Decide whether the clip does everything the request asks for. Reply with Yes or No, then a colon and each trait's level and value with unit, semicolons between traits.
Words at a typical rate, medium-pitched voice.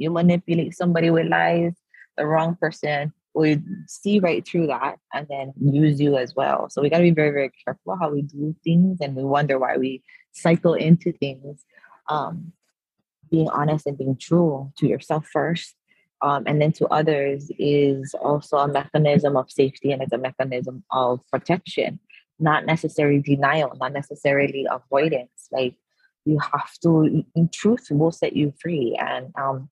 Yes: average, 170 wpm; medium, 150 Hz